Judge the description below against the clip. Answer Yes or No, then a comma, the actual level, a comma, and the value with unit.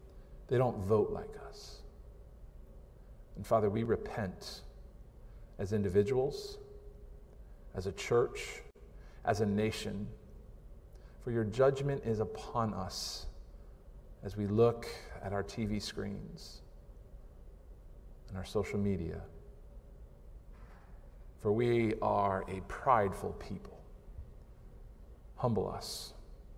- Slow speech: Yes, slow, 95 wpm